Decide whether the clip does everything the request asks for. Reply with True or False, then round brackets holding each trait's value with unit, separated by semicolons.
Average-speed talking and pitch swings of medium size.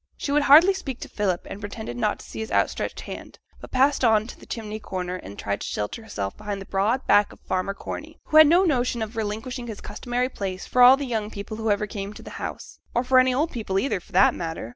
False (250 wpm; 4.5 semitones)